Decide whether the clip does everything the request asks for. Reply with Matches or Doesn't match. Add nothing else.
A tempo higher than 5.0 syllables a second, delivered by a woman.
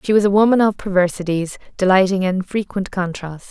Matches